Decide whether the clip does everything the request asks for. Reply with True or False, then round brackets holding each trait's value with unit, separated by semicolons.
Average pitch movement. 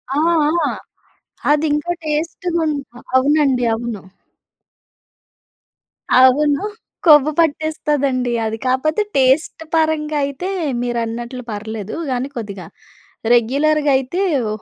True (4.1 semitones)